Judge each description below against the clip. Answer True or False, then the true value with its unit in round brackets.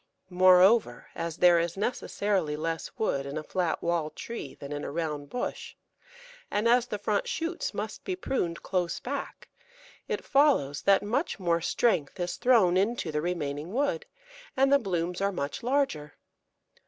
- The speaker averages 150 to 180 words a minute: True (160 wpm)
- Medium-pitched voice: True (180 Hz)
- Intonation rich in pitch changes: True (6.2 semitones)